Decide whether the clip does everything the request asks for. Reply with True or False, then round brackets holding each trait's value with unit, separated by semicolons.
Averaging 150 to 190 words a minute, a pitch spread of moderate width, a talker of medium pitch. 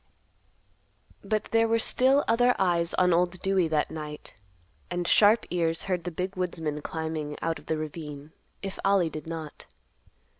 True (155 wpm; 3.6 semitones; 175 Hz)